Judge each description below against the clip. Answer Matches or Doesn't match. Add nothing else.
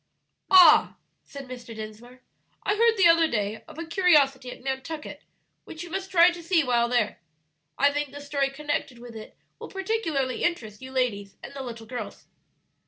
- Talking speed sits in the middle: Matches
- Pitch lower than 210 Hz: Doesn't match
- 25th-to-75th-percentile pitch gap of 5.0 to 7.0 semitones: Matches